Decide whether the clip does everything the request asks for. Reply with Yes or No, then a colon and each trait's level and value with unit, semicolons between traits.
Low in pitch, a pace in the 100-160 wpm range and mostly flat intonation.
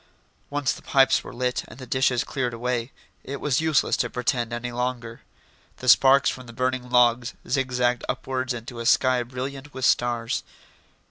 No: low, 125 Hz; average, 170 wpm; narrow, 1.6 semitones